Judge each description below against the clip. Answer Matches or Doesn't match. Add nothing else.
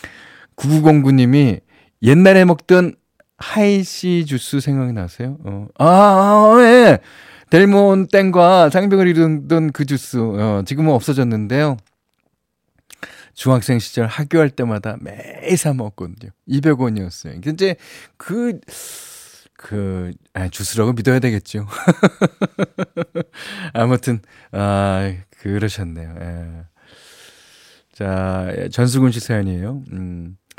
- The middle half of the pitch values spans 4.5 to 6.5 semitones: Doesn't match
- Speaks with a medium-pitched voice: Doesn't match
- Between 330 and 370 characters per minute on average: Doesn't match